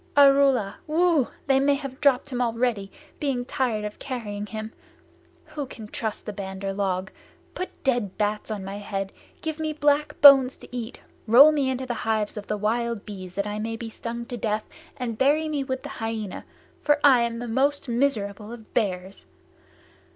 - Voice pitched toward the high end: Yes, high, 235 Hz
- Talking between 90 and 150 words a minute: No, average, 180 wpm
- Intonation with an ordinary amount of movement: Yes, average, 4.6 semitones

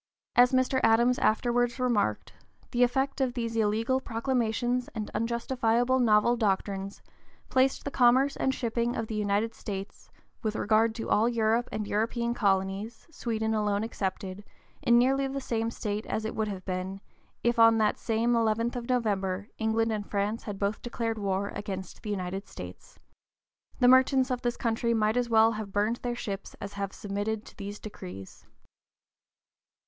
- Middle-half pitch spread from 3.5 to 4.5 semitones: No, average, 2.8 semitones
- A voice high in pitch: Yes, high, 225 Hz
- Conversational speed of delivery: Yes, average, 165 wpm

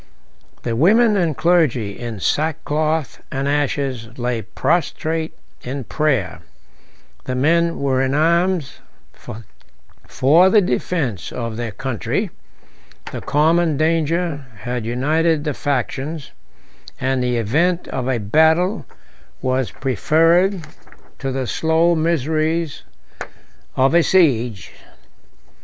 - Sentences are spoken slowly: Yes, slow, 105 wpm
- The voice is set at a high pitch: No, medium, 145 Hz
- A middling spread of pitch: Yes, average, 4.6 semitones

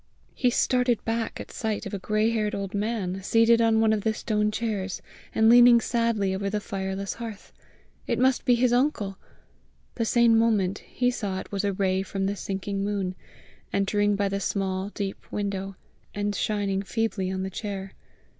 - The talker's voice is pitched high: Yes, high, 205 Hz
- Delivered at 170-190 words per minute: Yes, average, 180 wpm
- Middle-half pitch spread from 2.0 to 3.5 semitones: Yes, narrow, 2.6 semitones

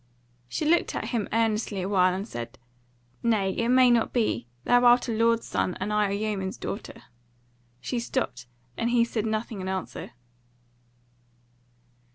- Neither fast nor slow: Yes, average, 155 wpm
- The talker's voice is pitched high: Yes, high, 215 Hz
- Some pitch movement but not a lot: Yes, average, 3.6 semitones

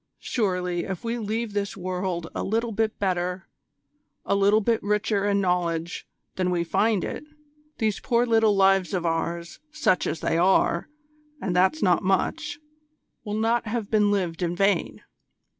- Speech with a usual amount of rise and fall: Yes, average, 3.4 semitones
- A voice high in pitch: Yes, high, 195 Hz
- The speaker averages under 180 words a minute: Yes, average, 160 wpm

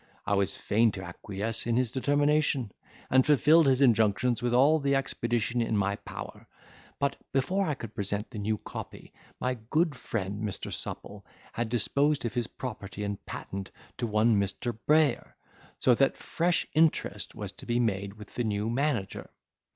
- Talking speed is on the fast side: No, average, 165 wpm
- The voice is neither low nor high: No, low, 120 Hz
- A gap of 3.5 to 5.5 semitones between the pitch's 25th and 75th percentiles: Yes, average, 4.9 semitones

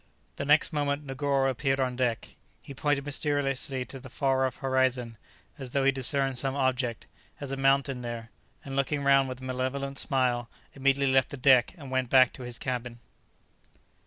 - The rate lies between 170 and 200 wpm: Yes, average, 180 wpm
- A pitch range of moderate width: No, narrow, 1.4 semitones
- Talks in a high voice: No, low, 135 Hz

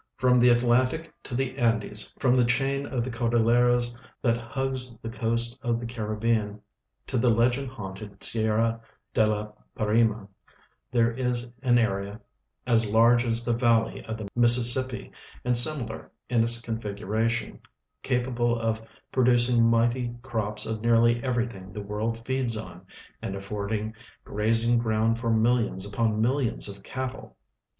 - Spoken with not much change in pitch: Yes, narrow, 1.7 semitones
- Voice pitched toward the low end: Yes, low, 115 Hz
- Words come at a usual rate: Yes, average, 145 wpm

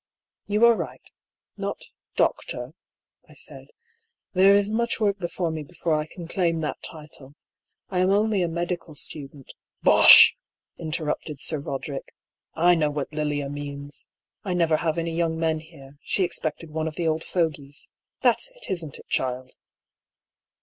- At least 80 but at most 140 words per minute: No, average, 170 wpm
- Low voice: No, medium, 160 Hz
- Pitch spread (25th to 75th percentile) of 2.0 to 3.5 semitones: Yes, average, 3.1 semitones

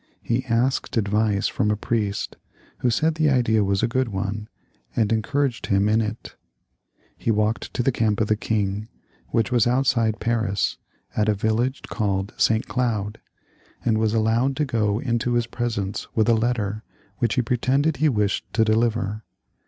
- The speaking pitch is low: Yes, low, 110 Hz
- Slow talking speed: No, average, 170 wpm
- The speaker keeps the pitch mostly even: Yes, narrow, 2.3 semitones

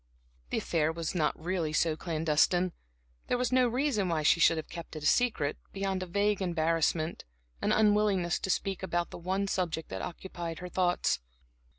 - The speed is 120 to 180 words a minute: Yes, average, 175 wpm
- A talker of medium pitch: Yes, medium, 175 Hz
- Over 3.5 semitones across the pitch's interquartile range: No, average, 3.2 semitones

